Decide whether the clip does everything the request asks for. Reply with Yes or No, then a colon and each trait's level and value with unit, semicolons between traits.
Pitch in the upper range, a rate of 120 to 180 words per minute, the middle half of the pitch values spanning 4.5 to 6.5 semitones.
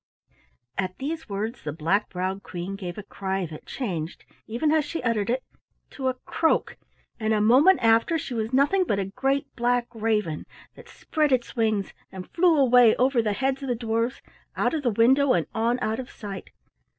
No: high, 230 Hz; average, 190 wpm; average, 5.0 semitones